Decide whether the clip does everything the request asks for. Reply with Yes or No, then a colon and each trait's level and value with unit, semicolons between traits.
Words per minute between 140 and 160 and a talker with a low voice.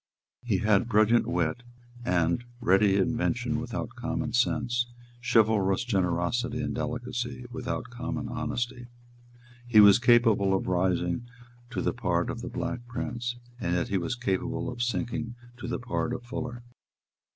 Yes: average, 145 wpm; low, 120 Hz